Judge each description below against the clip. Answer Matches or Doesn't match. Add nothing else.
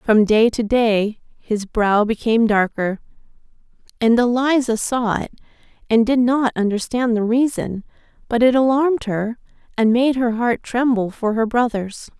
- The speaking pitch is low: Doesn't match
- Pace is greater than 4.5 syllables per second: Doesn't match